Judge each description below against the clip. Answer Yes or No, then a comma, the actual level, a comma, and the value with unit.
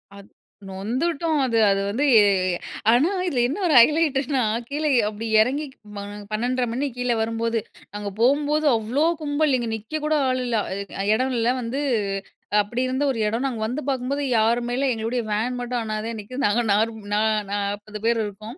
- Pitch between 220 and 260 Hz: Yes, high, 245 Hz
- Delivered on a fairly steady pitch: No, average, 4.0 semitones